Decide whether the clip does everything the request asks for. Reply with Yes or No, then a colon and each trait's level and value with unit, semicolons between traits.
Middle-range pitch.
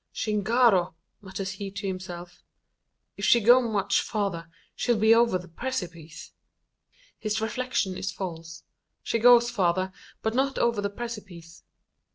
No: high, 200 Hz